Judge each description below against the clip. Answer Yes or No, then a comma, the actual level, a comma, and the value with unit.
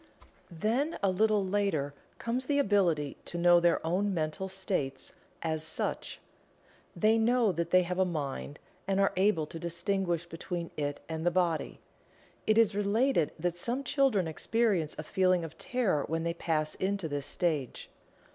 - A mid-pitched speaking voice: Yes, medium, 180 Hz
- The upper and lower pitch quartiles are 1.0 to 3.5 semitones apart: No, average, 4.2 semitones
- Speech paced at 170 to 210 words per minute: No, average, 160 wpm